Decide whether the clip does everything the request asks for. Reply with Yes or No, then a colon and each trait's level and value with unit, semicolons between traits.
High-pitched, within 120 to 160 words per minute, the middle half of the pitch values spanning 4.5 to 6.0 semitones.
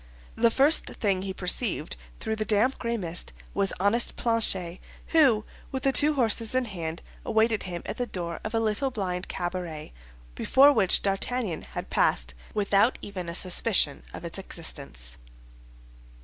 Yes: high, 205 Hz; average, 155 wpm; average, 4.8 semitones